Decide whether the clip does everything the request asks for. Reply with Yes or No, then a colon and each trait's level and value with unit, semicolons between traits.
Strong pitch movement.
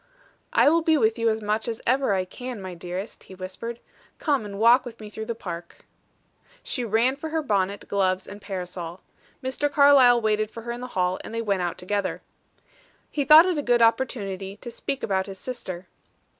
No: average, 4.7 semitones